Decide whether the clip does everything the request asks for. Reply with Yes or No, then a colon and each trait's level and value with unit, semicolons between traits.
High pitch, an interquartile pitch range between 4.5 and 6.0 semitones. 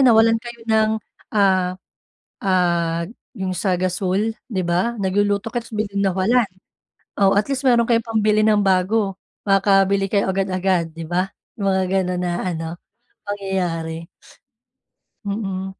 No: high, 195 Hz; narrow, 2.6 semitones